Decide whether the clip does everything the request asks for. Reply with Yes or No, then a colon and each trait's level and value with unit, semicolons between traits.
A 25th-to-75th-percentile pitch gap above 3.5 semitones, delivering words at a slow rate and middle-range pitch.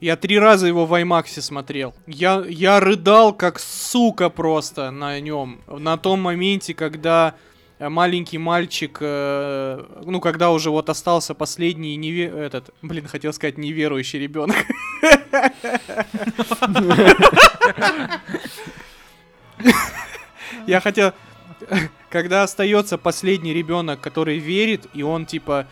Yes: average, 4.4 semitones; slow, 105 wpm; medium, 170 Hz